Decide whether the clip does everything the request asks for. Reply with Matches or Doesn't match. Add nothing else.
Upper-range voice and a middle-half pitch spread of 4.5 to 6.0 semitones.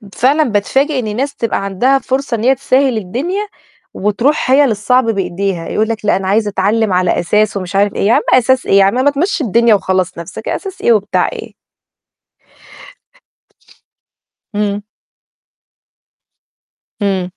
Matches